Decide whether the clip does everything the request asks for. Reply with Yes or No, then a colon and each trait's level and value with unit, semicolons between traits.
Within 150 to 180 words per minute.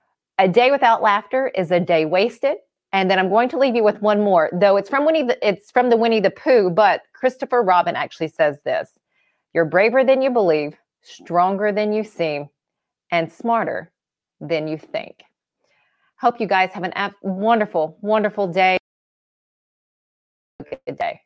Yes: average, 170 wpm